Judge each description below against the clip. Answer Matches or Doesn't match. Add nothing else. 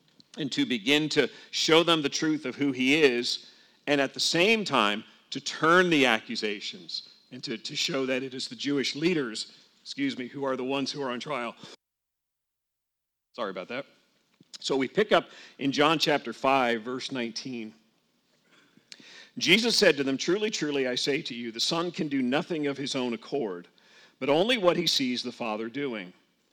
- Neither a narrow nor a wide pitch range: Matches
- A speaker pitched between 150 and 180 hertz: Doesn't match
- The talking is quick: Doesn't match